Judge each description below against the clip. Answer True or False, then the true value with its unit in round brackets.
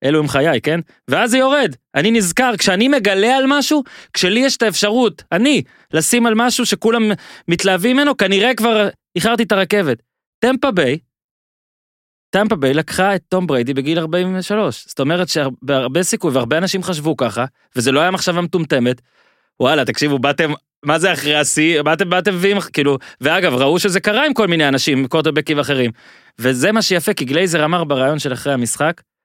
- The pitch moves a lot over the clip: True (6.4 semitones)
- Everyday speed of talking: False (170 wpm)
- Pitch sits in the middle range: True (180 Hz)